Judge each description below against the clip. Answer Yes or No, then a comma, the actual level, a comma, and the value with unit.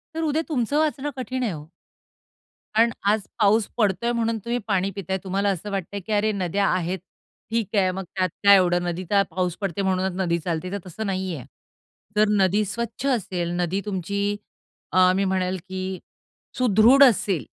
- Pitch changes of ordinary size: Yes, average, 3.0 semitones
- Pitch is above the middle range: Yes, high, 195 Hz